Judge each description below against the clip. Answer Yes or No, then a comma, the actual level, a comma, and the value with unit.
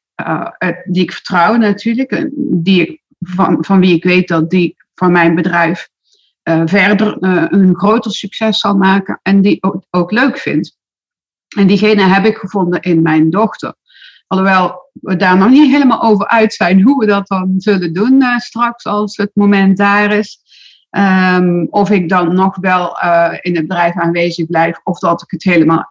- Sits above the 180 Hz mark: Yes, high, 190 Hz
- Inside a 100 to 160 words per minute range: No, average, 180 wpm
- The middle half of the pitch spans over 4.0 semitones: No, average, 3.3 semitones